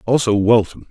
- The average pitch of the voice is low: Yes, low, 110 Hz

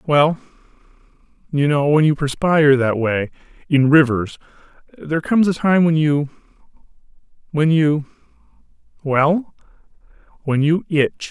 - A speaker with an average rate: No, slow, 105 wpm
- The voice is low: No, medium, 150 Hz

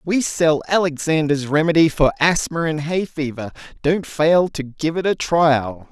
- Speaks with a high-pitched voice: No, medium, 155 Hz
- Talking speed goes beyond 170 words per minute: No, average, 160 wpm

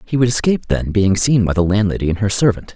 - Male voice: Yes, male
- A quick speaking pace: Yes, fast, 260 wpm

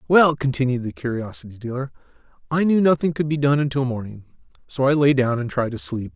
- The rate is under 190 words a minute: No, fast, 205 wpm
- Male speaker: Yes, male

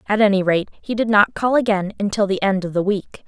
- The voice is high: Yes, high, 200 Hz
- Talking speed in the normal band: No, fast, 255 wpm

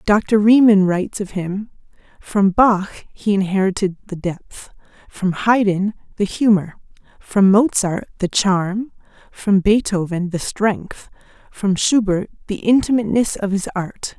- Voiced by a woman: Yes, female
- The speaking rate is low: Yes, slow, 125 wpm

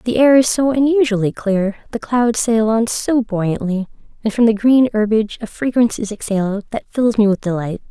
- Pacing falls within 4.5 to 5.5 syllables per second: Yes, 5.3 syllables/s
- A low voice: No, high, 220 Hz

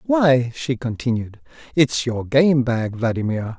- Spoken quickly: No, slow, 135 wpm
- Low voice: Yes, low, 130 Hz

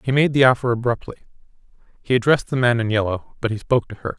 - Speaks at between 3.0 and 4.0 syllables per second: No, 7.2 syllables/s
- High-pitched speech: No, low, 120 Hz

